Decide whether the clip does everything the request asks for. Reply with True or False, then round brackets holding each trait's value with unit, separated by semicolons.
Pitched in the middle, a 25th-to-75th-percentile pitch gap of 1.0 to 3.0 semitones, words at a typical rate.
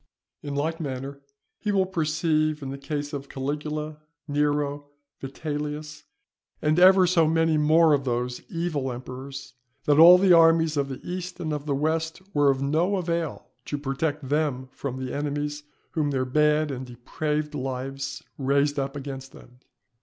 True (150 Hz; 2.5 semitones; 160 wpm)